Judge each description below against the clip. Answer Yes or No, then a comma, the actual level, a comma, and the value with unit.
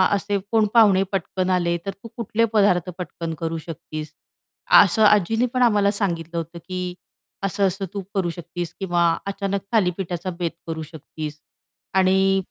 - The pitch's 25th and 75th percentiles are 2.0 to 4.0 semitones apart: Yes, average, 2.9 semitones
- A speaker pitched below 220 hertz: Yes, medium, 185 Hz